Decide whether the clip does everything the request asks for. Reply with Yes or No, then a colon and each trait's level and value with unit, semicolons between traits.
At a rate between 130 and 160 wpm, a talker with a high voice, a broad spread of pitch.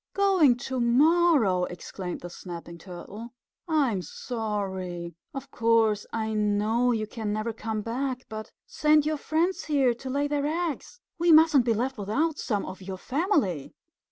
Yes: average, 155 wpm; high, 235 Hz; wide, 5.9 semitones